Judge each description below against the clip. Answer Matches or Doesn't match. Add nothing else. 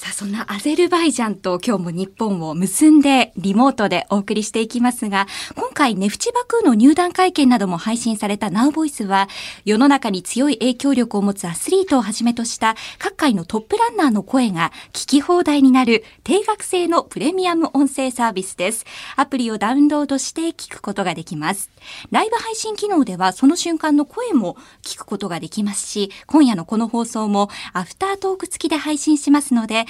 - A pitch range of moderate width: Doesn't match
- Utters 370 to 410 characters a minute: Matches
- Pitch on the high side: Matches